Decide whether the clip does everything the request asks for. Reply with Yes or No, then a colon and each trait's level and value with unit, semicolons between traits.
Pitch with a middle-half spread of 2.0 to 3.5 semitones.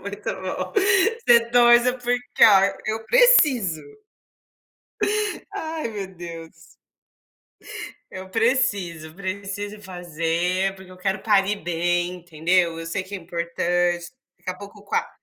No: average, 4.9 semitones